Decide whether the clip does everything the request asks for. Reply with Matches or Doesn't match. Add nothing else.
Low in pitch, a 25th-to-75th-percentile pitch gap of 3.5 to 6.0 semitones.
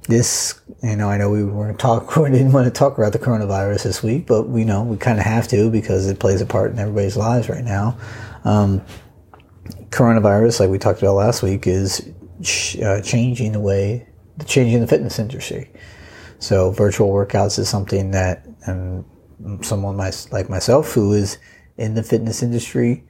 Doesn't match